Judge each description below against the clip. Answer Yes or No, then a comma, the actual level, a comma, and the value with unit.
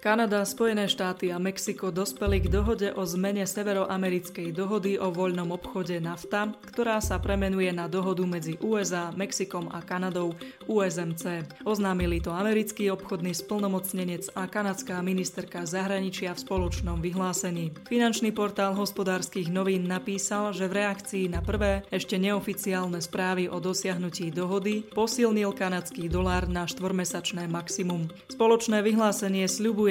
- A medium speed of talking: Yes, average, 130 wpm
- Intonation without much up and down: Yes, narrow, 2.2 semitones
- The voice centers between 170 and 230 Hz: Yes, high, 190 Hz